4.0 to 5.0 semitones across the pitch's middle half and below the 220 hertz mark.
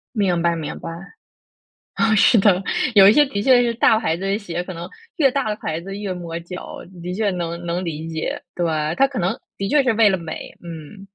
Yes: average, 4.3 semitones; high, 190 Hz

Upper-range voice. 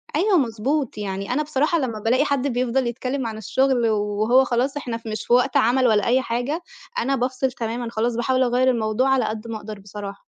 Yes: high, 245 Hz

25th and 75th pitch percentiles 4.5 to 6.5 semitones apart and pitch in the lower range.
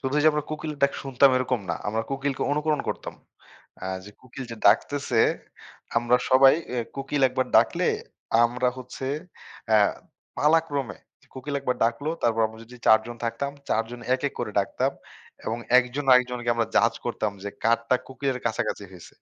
No: average, 3.0 semitones; low, 125 Hz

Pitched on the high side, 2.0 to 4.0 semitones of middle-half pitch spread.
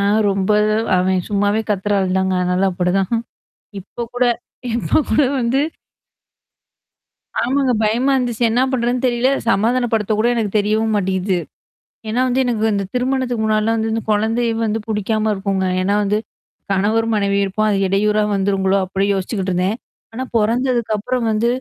Yes: high, 215 Hz; average, 3.3 semitones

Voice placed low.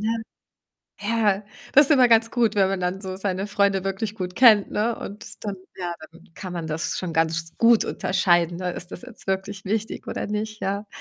No: high, 200 Hz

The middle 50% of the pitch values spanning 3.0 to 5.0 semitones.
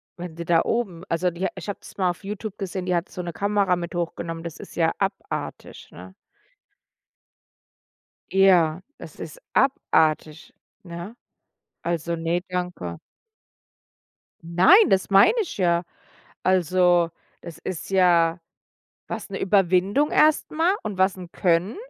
No: narrow, 2.5 semitones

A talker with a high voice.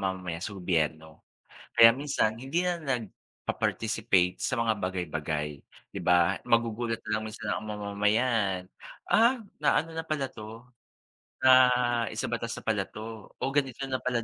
No: low, 110 Hz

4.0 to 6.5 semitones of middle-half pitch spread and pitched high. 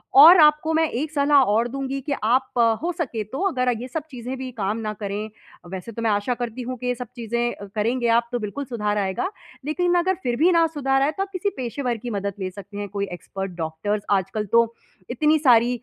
Yes: average, 5.0 semitones; high, 245 Hz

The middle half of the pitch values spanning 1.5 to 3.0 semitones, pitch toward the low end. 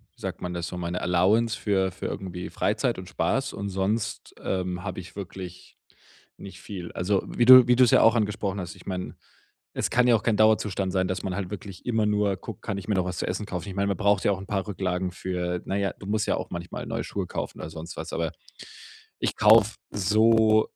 Yes: narrow, 2.6 semitones; very low, 95 Hz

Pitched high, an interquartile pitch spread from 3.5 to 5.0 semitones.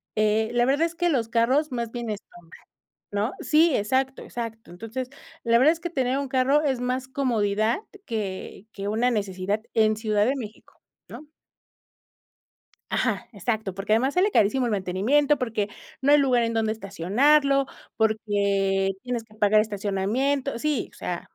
Yes: high, 230 Hz; average, 4.2 semitones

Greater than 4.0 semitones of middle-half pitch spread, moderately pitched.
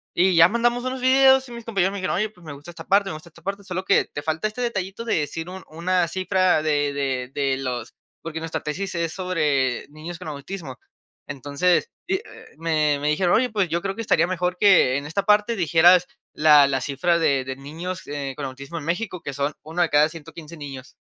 Yes: average, 4.7 semitones; medium, 170 Hz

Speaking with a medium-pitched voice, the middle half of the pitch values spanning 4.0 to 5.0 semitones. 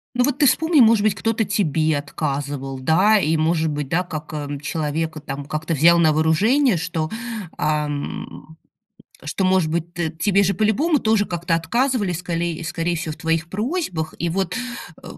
Yes: medium, 165 Hz; average, 4.5 semitones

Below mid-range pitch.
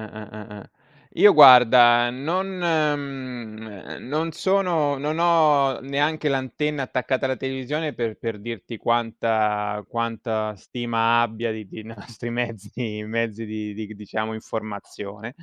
Yes: low, 120 Hz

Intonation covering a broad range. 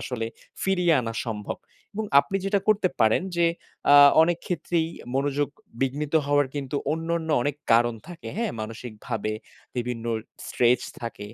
Yes: wide, 6.3 semitones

